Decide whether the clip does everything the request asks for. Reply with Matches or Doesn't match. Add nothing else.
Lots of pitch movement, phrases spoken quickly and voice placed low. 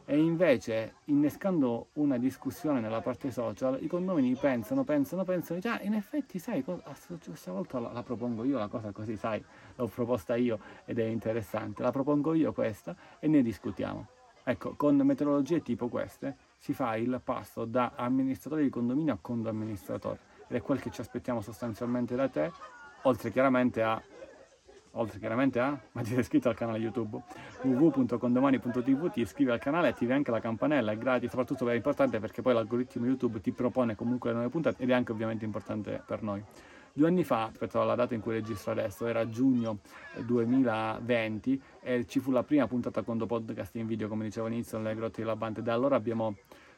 Doesn't match